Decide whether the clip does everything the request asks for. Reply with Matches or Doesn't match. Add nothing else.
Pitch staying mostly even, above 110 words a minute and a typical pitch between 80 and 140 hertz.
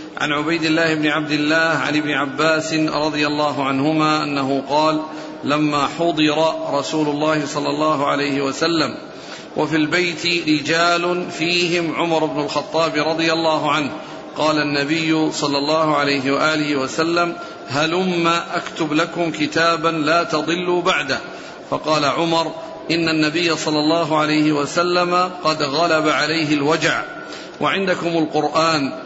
Doesn't match